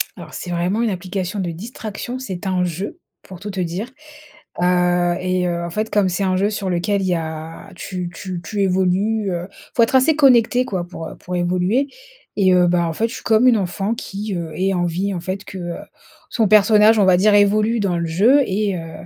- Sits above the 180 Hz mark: Yes, high, 190 Hz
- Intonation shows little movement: No, average, 3.2 semitones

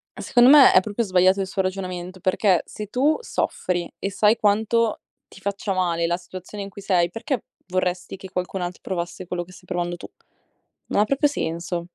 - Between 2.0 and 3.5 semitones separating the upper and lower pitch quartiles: Yes, average, 2.7 semitones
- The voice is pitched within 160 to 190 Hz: Yes, medium, 185 Hz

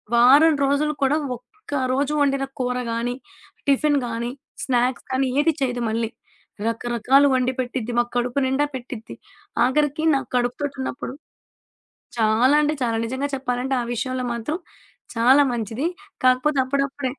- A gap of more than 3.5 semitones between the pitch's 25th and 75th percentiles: No, average, 2.7 semitones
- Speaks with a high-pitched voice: Yes, very high, 260 Hz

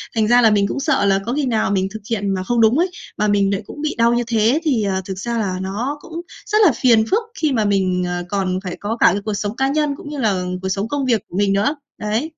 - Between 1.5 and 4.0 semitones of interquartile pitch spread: No, average, 4.8 semitones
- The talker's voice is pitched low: No, high, 220 Hz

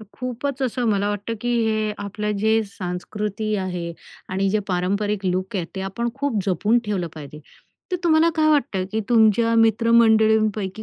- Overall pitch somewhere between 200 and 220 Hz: Yes, high, 215 Hz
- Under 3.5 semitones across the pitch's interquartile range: Yes, average, 3.0 semitones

